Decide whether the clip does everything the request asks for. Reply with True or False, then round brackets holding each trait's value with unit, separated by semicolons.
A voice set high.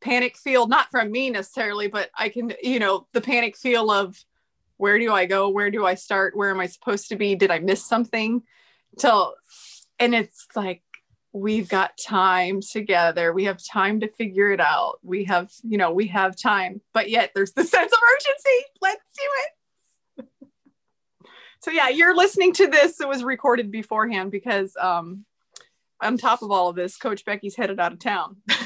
True (215 Hz)